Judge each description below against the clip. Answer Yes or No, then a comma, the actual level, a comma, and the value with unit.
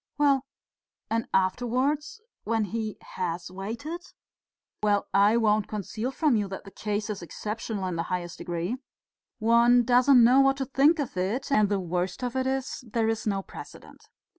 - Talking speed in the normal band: Yes, average, 165 wpm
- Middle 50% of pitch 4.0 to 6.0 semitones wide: Yes, average, 4.7 semitones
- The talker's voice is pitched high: Yes, high, 225 Hz